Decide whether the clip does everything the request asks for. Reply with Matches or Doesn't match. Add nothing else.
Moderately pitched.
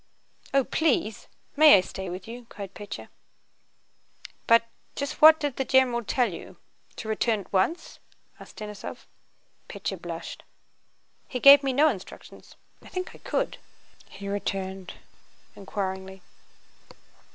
Doesn't match